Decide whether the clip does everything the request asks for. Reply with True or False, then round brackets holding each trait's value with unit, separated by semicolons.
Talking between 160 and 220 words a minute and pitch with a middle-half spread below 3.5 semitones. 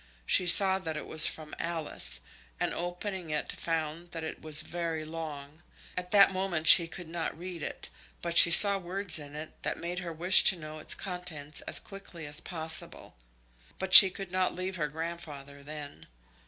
True (180 wpm; 2.7 semitones)